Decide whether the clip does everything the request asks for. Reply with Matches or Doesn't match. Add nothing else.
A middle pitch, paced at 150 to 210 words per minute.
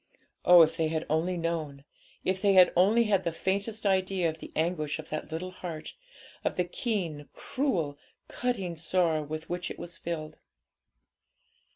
Matches